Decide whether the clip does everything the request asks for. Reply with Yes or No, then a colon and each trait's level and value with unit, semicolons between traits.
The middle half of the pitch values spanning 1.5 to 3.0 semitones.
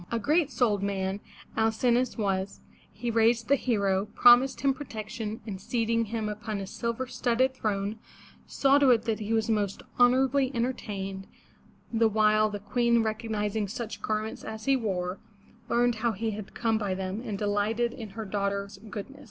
Yes: average, 2.7 semitones